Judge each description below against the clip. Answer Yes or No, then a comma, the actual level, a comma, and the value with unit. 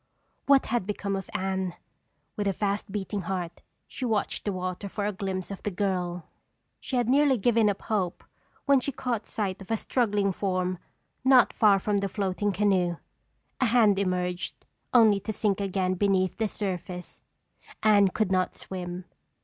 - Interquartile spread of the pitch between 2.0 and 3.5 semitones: Yes, narrow, 2.5 semitones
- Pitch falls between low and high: No, high, 200 Hz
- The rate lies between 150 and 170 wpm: Yes, average, 165 wpm